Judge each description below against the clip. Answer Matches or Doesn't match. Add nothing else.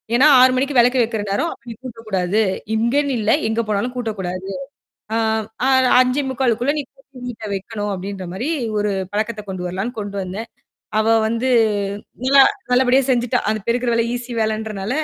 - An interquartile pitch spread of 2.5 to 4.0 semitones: Matches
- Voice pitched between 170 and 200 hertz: Doesn't match